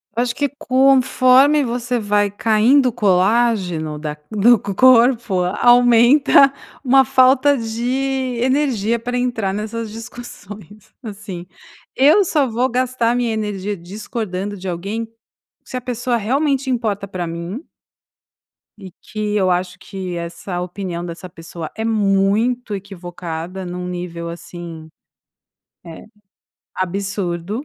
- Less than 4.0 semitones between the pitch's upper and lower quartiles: No, average, 5.1 semitones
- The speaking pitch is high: Yes, high, 215 Hz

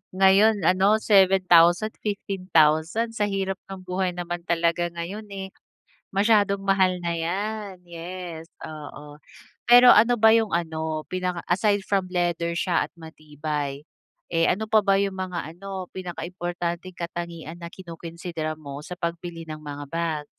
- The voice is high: No, medium, 175 Hz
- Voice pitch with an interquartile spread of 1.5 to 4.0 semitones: Yes, average, 2.8 semitones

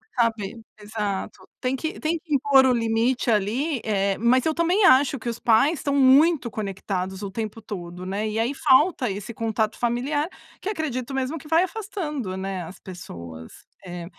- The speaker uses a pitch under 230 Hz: No, high, 235 Hz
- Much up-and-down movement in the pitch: Yes, wide, 6.0 semitones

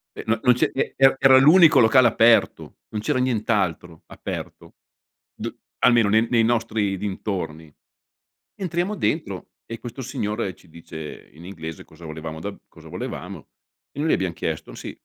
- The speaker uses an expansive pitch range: Yes, wide, 6.5 semitones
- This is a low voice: Yes, low, 110 Hz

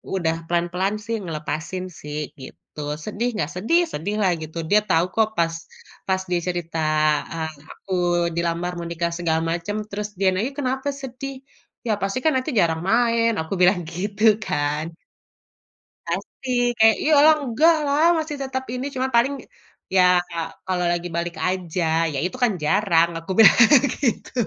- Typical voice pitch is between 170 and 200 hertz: Yes, high, 190 Hz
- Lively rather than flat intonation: Yes, wide, 6.0 semitones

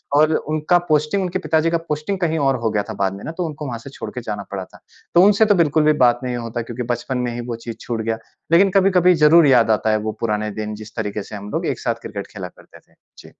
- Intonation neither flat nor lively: No, wide, 6.4 semitones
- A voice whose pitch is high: No, low, 125 Hz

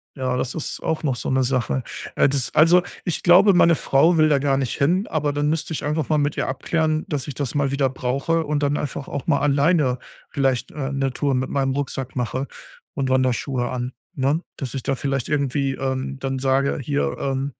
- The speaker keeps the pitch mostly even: Yes, narrow, 2.1 semitones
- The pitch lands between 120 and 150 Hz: Yes, medium, 140 Hz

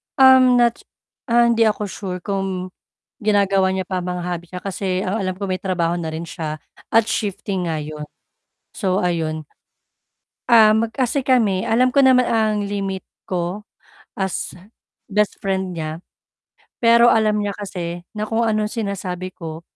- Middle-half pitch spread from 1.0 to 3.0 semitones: No, average, 3.6 semitones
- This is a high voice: Yes, high, 195 Hz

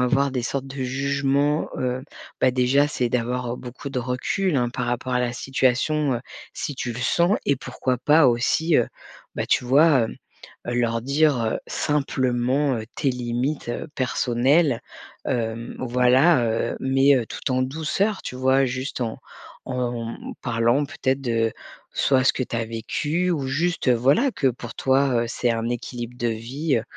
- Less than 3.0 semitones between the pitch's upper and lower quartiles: Yes, narrow, 2.6 semitones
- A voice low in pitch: Yes, low, 130 Hz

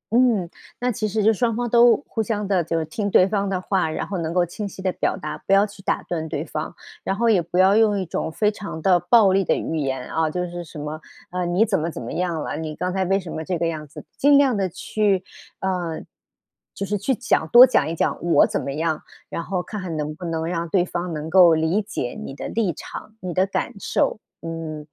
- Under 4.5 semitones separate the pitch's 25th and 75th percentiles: Yes, average, 3.9 semitones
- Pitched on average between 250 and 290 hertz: No, medium, 185 Hz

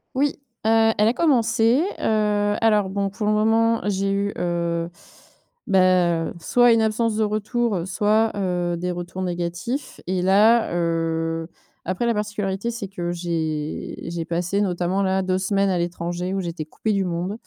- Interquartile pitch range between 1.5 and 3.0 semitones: No, average, 3.8 semitones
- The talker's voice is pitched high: Yes, high, 195 Hz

